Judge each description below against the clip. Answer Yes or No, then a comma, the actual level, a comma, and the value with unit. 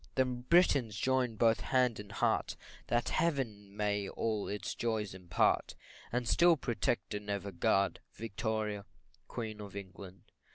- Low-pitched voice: Yes, low, 110 Hz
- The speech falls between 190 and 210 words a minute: No, slow, 135 wpm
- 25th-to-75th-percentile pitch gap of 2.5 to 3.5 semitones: Yes, average, 3.2 semitones